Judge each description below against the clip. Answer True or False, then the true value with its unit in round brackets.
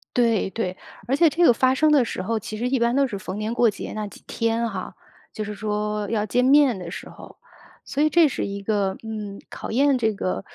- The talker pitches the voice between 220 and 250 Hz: True (225 Hz)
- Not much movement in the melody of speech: False (3.8 semitones)